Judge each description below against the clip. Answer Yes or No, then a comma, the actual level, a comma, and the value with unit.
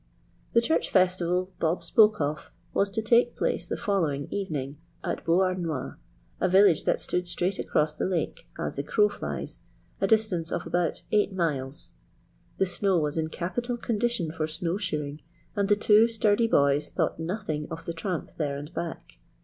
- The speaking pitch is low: No, medium, 180 Hz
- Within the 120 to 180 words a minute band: Yes, average, 170 wpm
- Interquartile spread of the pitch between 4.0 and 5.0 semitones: Yes, average, 4.7 semitones